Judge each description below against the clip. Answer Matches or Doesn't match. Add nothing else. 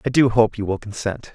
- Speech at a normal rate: Doesn't match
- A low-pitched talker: Matches